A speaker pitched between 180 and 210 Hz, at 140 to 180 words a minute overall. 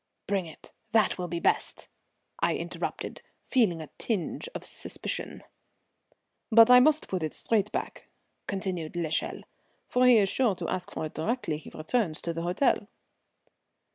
Yes: high, 190 Hz; average, 155 wpm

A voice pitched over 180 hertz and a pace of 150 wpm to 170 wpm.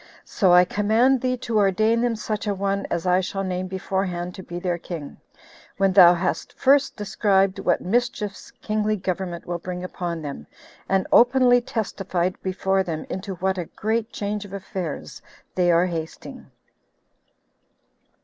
Yes: high, 190 Hz; average, 155 wpm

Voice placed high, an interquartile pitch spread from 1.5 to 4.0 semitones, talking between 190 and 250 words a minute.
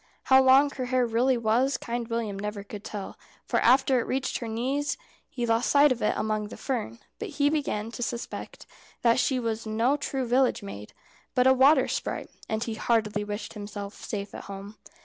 Yes: high, 235 Hz; average, 3.5 semitones; average, 195 wpm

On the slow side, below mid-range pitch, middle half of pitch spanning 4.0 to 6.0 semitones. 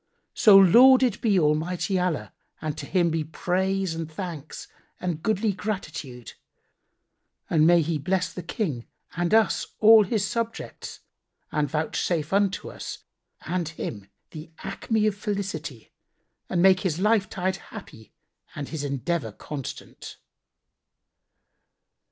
No: slow, 125 wpm; medium, 180 Hz; average, 4.3 semitones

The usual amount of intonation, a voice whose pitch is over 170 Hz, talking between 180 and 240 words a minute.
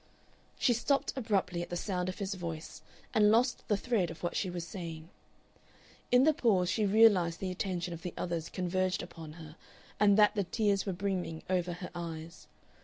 Yes: average, 3.2 semitones; medium, 185 Hz; average, 185 wpm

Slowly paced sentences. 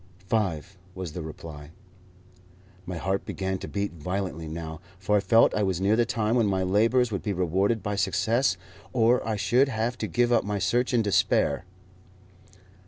No: average, 175 wpm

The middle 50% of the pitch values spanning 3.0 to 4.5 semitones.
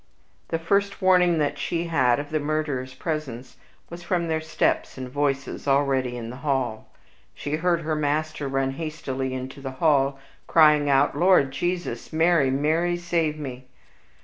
Yes: average, 3.5 semitones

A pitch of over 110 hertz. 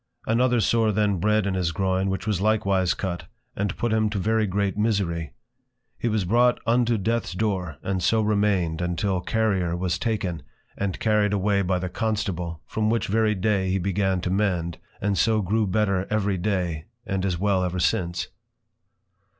No: low, 100 Hz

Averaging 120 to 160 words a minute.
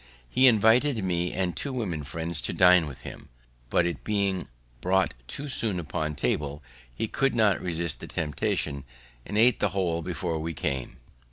No: average, 170 wpm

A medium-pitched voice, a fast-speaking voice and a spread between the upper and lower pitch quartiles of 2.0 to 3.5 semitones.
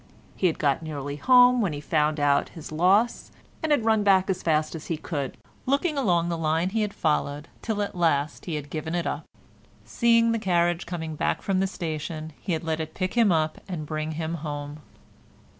No: medium, 165 Hz; fast, 210 wpm; average, 4.1 semitones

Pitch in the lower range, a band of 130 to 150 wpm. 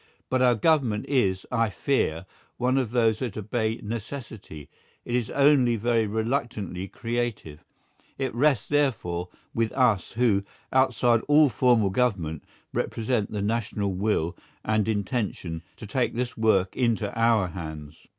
Yes: low, 115 Hz; slow, 135 wpm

